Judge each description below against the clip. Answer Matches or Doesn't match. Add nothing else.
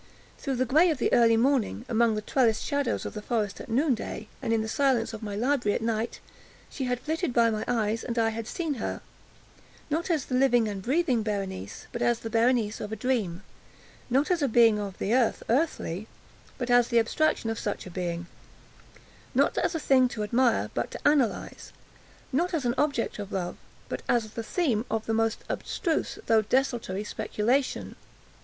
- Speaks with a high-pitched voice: Matches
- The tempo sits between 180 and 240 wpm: Matches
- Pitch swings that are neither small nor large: Matches